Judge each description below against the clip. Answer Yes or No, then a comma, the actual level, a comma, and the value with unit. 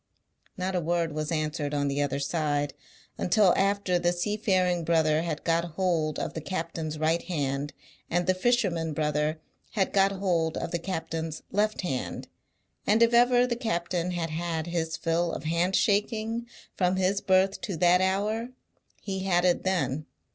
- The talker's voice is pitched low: No, medium, 175 Hz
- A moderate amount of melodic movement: Yes, average, 3.2 semitones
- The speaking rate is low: No, average, 165 wpm